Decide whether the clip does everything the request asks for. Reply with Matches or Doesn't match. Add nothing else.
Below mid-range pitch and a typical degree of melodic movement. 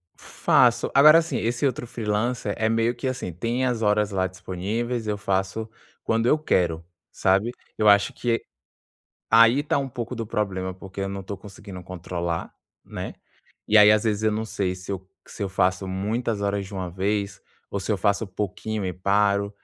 Matches